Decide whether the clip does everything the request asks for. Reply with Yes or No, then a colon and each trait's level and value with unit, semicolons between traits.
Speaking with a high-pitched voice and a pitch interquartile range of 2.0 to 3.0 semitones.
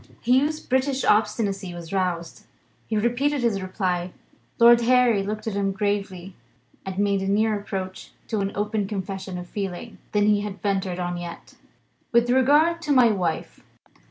No: high, 205 Hz; average, 3.8 semitones